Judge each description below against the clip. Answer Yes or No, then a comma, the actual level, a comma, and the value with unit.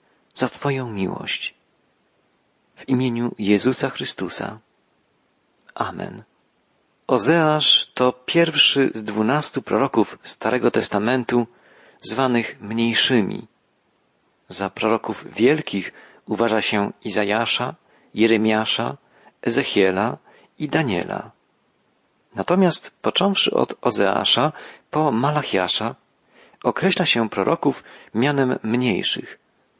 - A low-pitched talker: Yes, low, 120 Hz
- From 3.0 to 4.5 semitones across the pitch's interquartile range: Yes, average, 3.6 semitones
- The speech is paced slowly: Yes, slow, 80 wpm